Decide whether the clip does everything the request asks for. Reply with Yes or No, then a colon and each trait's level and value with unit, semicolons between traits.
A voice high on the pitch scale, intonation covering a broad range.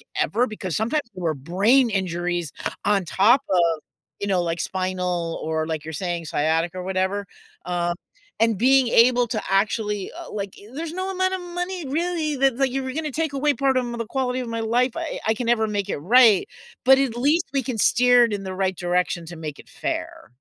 Yes: high, 220 Hz; wide, 6.7 semitones